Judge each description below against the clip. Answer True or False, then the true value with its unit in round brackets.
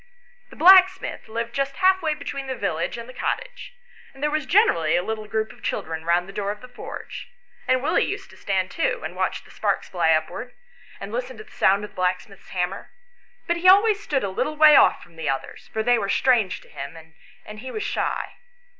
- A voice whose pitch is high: True (235 Hz)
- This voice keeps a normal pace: False (220 wpm)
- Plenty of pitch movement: True (8.6 semitones)